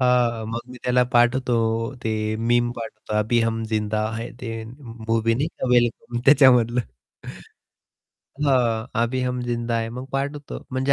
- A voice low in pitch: Yes, low, 120 Hz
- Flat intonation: Yes, narrow, 1.9 semitones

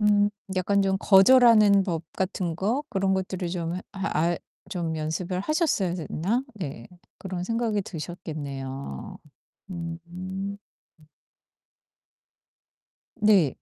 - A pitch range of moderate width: Yes, average, 3.2 semitones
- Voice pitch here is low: No, medium, 185 Hz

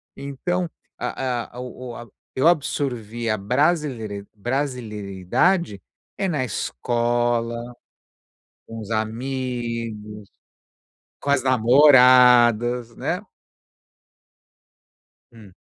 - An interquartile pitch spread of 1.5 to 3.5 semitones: Yes, average, 2.9 semitones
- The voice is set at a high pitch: No, low, 120 Hz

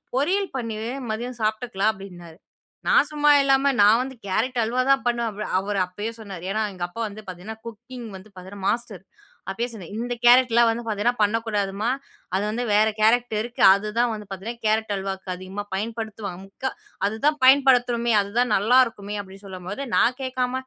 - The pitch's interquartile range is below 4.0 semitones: Yes, average, 3.4 semitones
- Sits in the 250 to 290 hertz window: No, high, 220 Hz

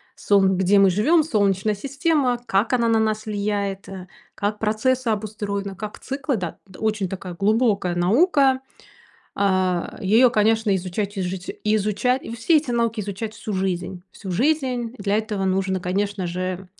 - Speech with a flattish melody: No, average, 3.2 semitones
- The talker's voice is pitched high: Yes, high, 210 Hz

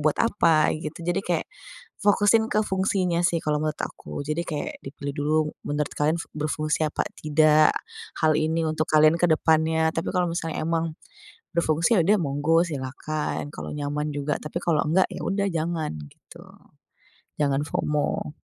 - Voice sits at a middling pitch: Yes, medium, 155 Hz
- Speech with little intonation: Yes, narrow, 2.1 semitones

